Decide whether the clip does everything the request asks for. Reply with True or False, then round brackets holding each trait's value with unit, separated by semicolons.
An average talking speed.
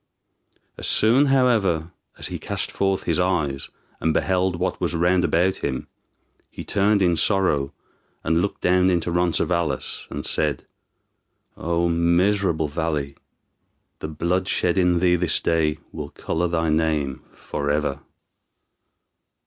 False (130 wpm)